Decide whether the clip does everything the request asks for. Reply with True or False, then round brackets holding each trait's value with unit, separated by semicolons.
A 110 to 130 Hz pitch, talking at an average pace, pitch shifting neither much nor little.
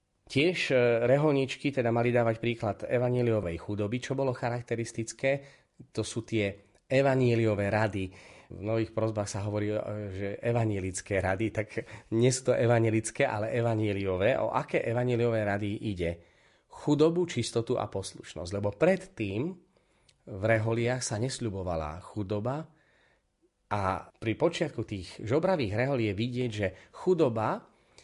True (115 Hz; 120 wpm; 3.3 semitones)